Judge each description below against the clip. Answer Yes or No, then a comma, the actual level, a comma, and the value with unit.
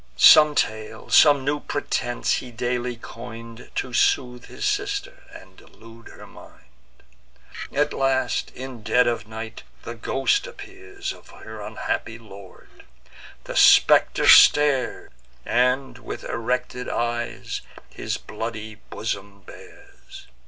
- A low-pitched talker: Yes, low, 125 Hz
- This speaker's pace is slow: Yes, slow, 115 wpm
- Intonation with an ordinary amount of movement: Yes, average, 4.1 semitones